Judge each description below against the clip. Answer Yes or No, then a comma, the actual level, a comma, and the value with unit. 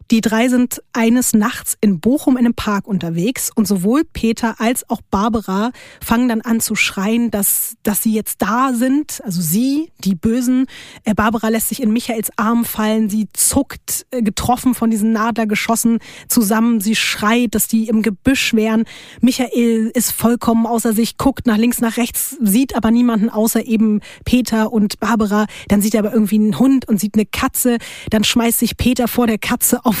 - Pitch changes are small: Yes, narrow, 1.9 semitones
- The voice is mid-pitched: No, high, 230 Hz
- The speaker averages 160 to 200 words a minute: Yes, average, 180 wpm